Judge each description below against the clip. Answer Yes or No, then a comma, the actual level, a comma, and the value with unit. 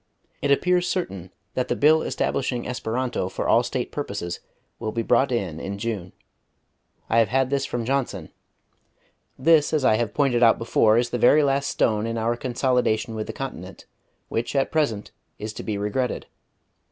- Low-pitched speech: Yes, low, 120 Hz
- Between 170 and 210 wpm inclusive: Yes, average, 175 wpm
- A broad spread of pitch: No, average, 4.0 semitones